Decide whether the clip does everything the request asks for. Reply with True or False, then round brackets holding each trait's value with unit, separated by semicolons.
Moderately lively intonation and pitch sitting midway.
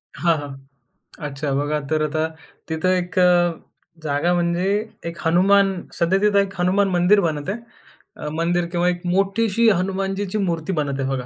True (3.5 semitones; 175 Hz)